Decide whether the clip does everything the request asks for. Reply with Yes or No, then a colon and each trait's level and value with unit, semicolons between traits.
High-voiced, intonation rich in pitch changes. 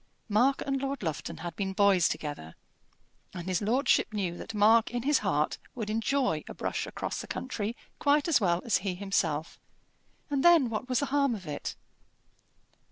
Yes: high, 215 Hz; wide, 6.6 semitones